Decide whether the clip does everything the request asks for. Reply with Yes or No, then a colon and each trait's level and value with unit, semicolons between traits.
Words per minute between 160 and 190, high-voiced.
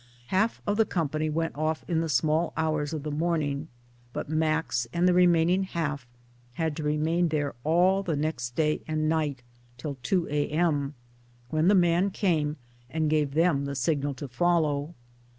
No: average, 170 wpm; medium, 155 Hz